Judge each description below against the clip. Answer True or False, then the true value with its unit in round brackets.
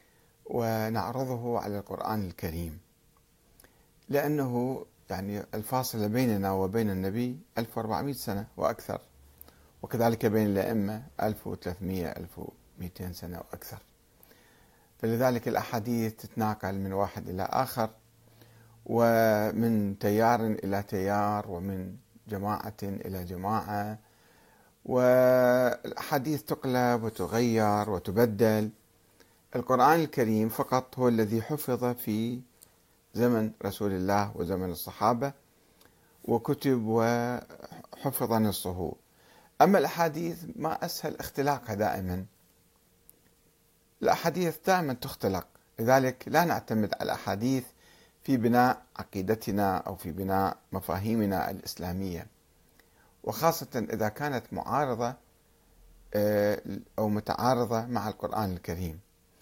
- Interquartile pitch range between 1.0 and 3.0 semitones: False (3.9 semitones)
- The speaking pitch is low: True (110 Hz)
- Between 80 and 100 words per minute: True (85 wpm)